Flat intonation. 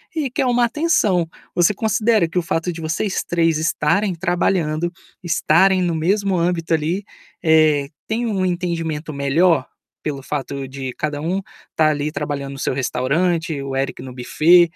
No: average, 3.6 semitones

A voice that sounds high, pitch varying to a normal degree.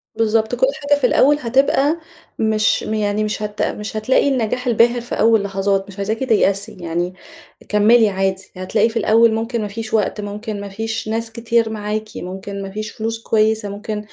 No: high, 215 Hz; narrow, 1.9 semitones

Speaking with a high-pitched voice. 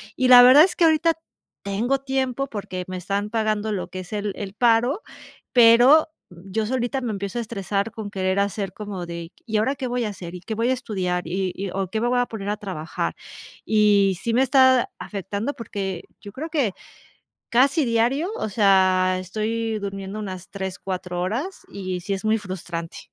Yes: high, 210 Hz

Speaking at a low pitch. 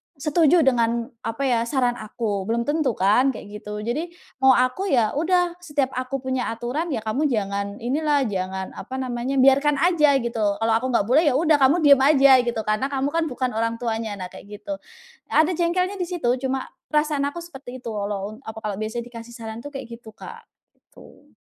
No: very high, 255 Hz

